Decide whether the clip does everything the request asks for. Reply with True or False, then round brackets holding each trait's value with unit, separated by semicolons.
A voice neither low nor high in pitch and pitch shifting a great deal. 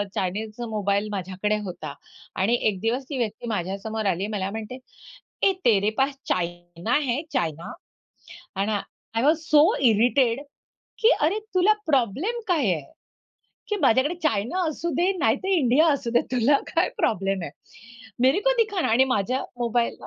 False (235 Hz; 6.1 semitones)